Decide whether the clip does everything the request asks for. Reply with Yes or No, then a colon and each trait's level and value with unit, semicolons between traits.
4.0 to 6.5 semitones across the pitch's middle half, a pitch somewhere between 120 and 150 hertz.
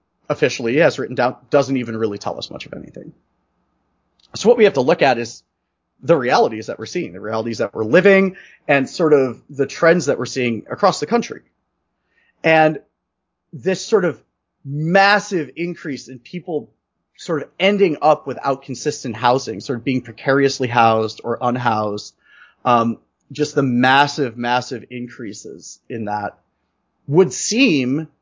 Yes: average, 5.0 semitones; low, 135 Hz